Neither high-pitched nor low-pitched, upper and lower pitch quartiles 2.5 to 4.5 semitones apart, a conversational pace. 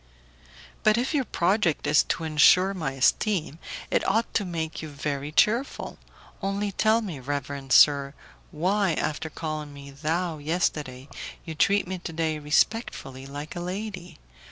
No: medium, 160 Hz; average, 5.1 semitones; average, 145 wpm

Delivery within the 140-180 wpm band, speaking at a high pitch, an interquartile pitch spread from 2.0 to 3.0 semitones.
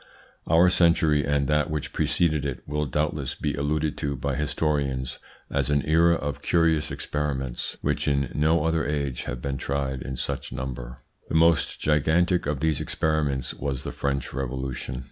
No: average, 165 wpm; very low, 75 Hz; narrow, 2.4 semitones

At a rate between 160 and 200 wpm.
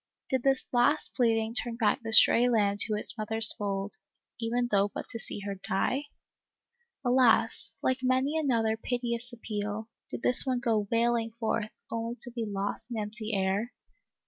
Yes: average, 165 wpm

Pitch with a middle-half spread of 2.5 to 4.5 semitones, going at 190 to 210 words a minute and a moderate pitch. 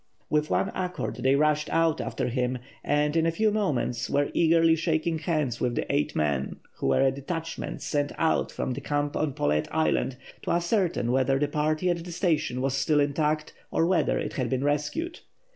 Yes: average, 3.6 semitones; average, 195 wpm; medium, 150 Hz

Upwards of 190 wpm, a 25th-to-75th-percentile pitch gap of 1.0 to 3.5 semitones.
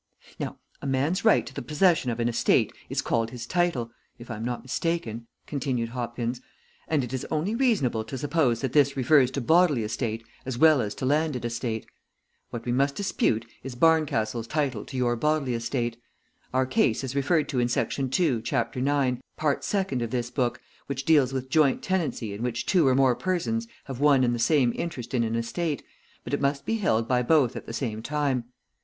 No: average, 200 wpm; average, 4.2 semitones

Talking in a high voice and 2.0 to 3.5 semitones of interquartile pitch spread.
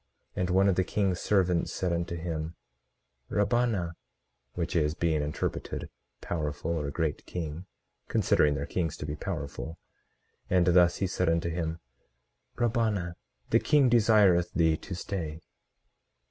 No: very low, 85 Hz; average, 2.9 semitones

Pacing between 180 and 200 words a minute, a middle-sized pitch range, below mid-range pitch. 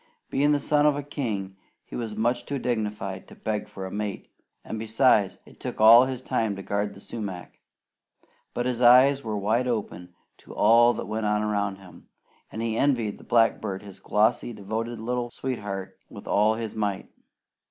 Yes: average, 185 wpm; average, 3.0 semitones; low, 110 Hz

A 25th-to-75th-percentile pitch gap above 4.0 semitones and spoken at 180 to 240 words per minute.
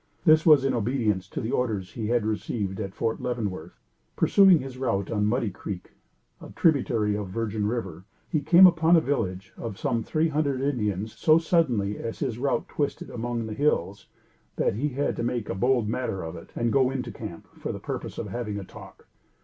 Yes: average, 4.8 semitones; average, 200 wpm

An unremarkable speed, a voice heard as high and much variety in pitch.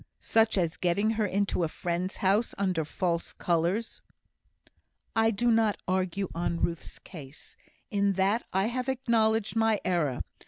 No: average, 145 wpm; high, 195 Hz; average, 4.3 semitones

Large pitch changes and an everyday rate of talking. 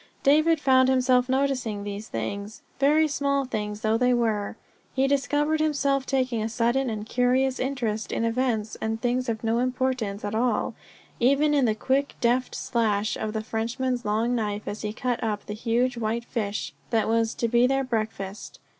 No: average, 3.2 semitones; average, 170 wpm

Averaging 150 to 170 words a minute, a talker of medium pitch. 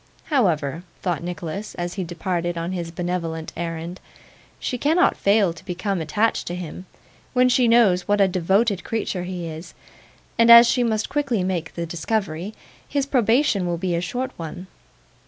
Yes: average, 165 wpm; medium, 180 Hz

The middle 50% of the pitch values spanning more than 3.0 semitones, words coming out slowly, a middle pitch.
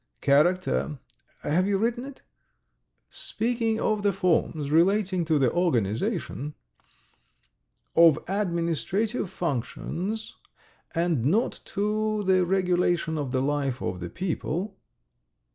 Yes: wide, 5.5 semitones; slow, 105 wpm; medium, 175 Hz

